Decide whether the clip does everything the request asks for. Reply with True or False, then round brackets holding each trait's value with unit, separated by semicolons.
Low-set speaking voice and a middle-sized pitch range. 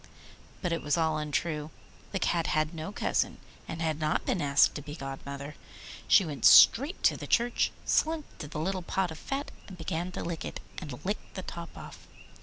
False (165 Hz; 3.6 semitones)